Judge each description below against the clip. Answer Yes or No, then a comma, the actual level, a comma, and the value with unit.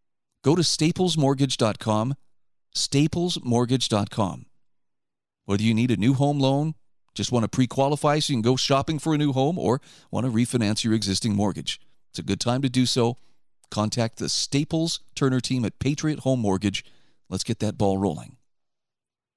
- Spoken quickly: No, average, 165 wpm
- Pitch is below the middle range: Yes, low, 125 Hz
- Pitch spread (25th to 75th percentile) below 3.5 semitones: No, average, 4.3 semitones